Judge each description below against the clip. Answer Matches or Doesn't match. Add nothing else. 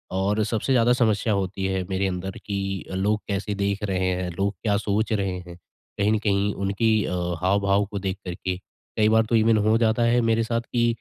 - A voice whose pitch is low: Matches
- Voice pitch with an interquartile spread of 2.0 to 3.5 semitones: Matches